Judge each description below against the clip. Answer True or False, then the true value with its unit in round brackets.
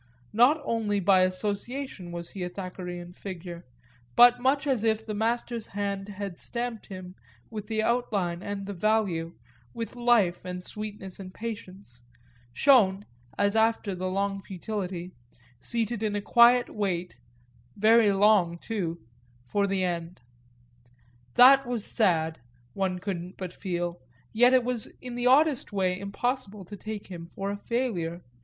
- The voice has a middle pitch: False (200 Hz)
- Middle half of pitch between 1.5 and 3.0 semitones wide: False (3.9 semitones)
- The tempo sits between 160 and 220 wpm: False (145 wpm)